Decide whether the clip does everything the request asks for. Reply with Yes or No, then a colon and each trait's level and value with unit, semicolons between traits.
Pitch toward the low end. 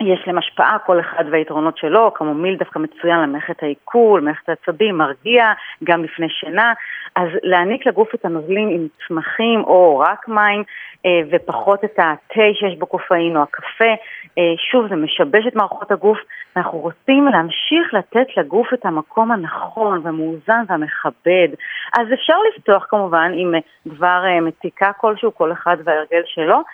No: medium, 180 Hz